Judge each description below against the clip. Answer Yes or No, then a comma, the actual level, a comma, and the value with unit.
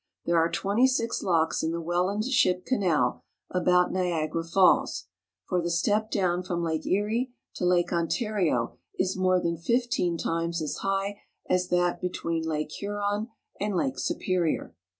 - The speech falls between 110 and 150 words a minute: No, average, 160 wpm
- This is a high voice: No, medium, 180 Hz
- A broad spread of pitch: No, average, 3.3 semitones